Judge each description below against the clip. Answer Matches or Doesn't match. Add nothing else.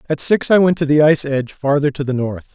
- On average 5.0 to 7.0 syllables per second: Matches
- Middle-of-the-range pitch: Matches